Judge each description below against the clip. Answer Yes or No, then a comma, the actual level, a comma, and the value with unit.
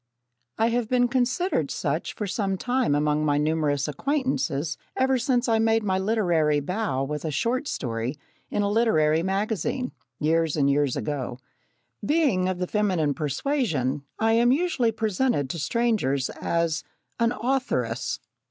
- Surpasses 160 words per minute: No, average, 145 wpm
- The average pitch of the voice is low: No, high, 190 Hz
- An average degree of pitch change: No, wide, 8.2 semitones